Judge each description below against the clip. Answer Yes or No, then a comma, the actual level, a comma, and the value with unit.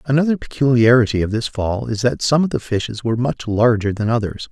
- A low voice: Yes, low, 120 Hz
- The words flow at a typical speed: No, fast, 215 wpm